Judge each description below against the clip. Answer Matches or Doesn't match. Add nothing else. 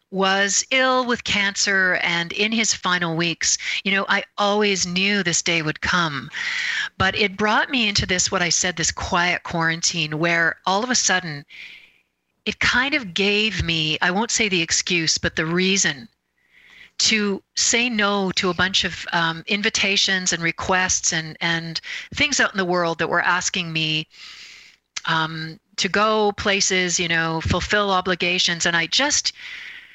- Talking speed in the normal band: Matches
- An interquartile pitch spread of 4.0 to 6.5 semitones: Doesn't match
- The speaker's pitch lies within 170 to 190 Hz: Matches